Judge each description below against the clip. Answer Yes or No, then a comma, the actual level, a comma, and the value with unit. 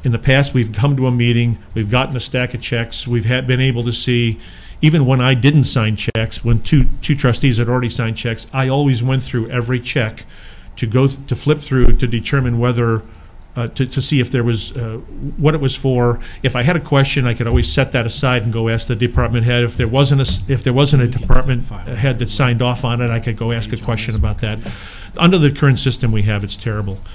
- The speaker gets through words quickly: Yes, fast, 240 wpm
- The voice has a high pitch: No, low, 125 Hz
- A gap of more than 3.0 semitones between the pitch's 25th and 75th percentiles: No, narrow, 2.5 semitones